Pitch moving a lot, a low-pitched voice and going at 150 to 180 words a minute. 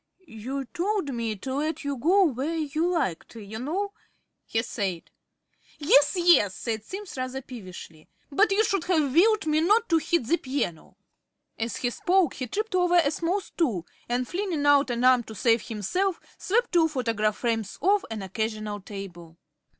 No: wide, 7.8 semitones; very high, 275 Hz; average, 170 wpm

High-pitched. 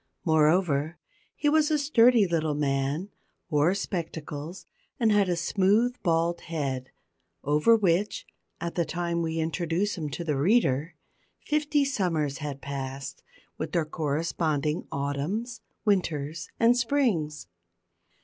No: medium, 170 Hz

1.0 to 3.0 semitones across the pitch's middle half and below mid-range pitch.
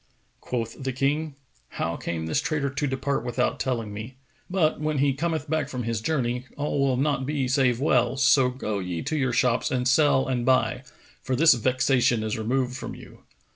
Yes: narrow, 2.6 semitones; low, 130 Hz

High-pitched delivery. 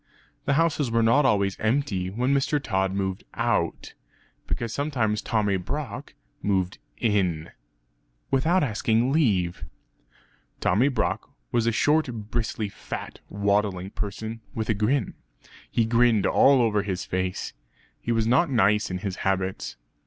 No: low, 110 Hz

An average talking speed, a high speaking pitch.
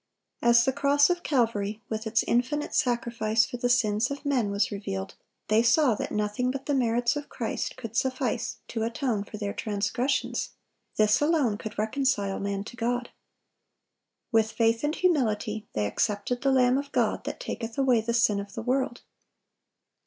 Yes: average, 170 wpm; high, 235 Hz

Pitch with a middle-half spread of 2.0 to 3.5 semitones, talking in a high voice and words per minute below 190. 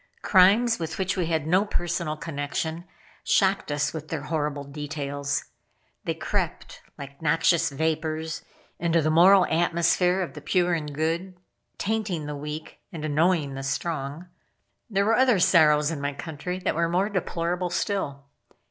No: average, 3.2 semitones; medium, 165 Hz; average, 150 wpm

